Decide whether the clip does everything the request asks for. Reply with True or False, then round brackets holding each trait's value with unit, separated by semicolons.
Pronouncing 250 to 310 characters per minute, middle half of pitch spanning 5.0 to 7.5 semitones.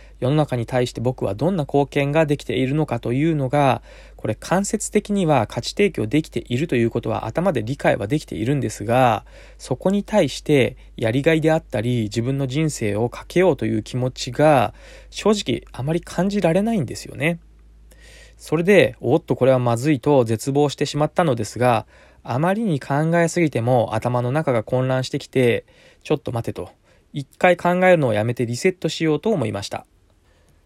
False (365 characters per minute; 5.3 semitones)